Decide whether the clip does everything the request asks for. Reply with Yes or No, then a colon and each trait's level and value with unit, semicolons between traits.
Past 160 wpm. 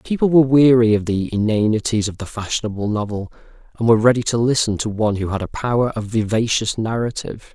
Yes: average, 190 wpm